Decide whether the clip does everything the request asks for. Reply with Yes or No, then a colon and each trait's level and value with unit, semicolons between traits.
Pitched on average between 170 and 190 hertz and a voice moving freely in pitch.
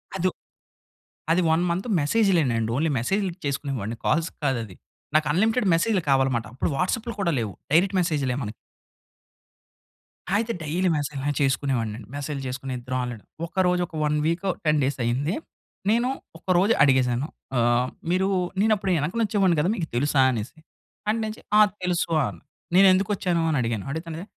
No: medium, 155 Hz; wide, 6.2 semitones